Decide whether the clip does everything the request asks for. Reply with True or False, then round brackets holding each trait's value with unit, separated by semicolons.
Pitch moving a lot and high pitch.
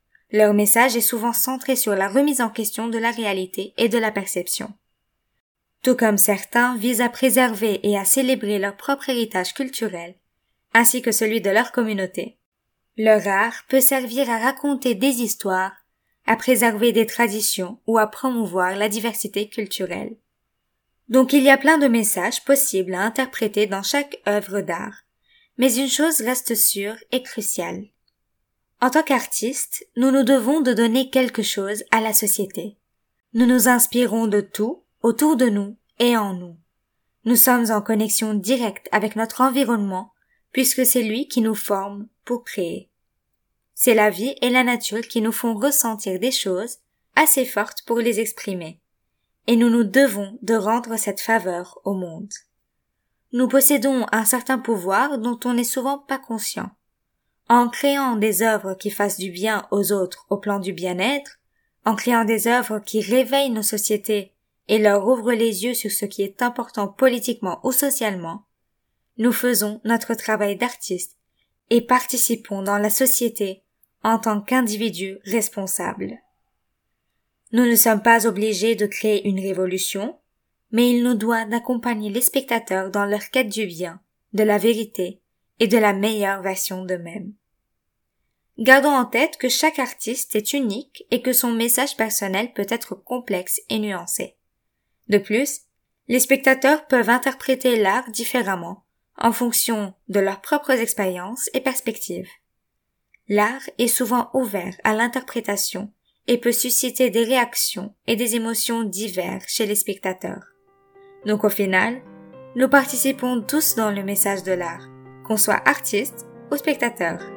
False (3.5 semitones; 230 Hz)